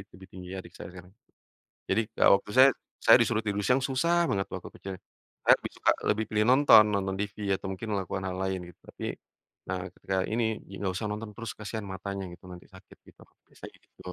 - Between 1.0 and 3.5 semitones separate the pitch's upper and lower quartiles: Yes, narrow, 2.5 semitones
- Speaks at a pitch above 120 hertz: No, low, 100 Hz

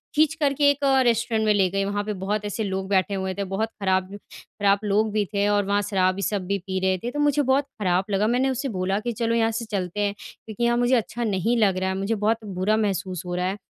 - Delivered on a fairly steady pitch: No, average, 3.2 semitones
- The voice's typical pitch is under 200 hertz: No, high, 205 Hz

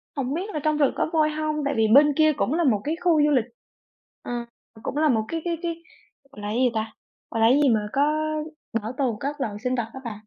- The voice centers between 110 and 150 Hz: No, very high, 280 Hz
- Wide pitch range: No, average, 4.9 semitones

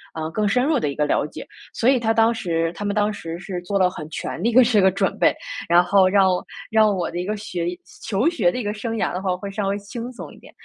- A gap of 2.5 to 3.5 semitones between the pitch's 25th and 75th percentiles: No, average, 3.9 semitones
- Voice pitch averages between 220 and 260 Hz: No, high, 200 Hz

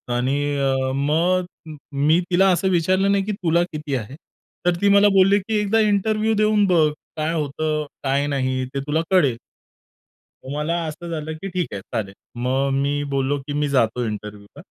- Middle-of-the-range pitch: Yes, medium, 155 Hz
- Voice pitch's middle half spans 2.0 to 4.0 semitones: No, wide, 5.4 semitones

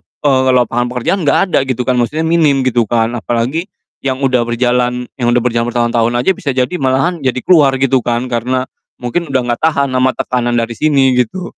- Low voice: Yes, low, 130 Hz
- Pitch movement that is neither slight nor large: No, narrow, 2.3 semitones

